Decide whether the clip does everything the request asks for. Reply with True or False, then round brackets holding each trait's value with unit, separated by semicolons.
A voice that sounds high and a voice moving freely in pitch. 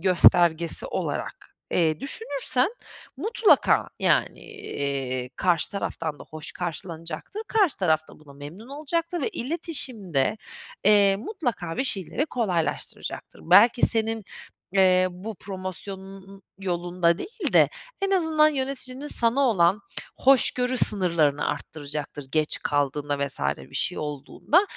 True (195 Hz; 8.3 semitones)